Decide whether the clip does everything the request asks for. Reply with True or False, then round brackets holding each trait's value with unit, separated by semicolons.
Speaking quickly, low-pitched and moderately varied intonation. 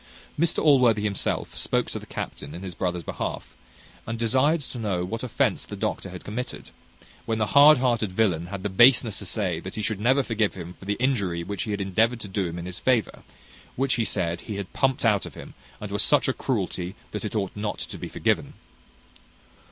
True (215 wpm; 105 Hz; 4.2 semitones)